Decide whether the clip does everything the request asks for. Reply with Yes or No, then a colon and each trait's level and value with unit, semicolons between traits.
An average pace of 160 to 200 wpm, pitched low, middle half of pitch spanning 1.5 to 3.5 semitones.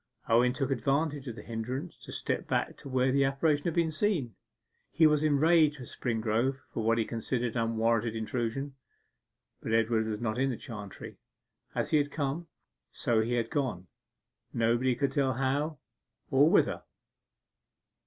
No: average, 165 wpm; low, 130 Hz; average, 4.0 semitones